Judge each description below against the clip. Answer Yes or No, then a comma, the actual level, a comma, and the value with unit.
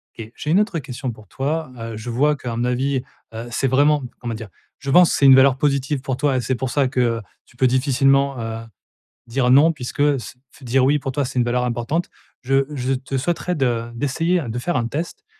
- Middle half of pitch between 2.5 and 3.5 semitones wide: Yes, average, 2.8 semitones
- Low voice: Yes, low, 130 Hz